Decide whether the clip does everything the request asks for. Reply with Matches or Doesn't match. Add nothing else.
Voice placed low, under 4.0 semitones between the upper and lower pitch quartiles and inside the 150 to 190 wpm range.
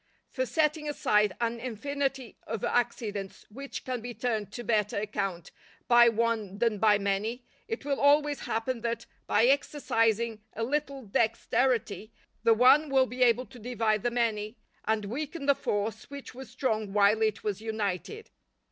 Doesn't match